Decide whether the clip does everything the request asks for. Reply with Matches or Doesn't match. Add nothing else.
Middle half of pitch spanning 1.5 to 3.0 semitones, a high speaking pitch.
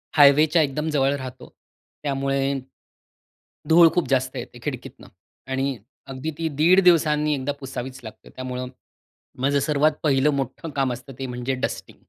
Doesn't match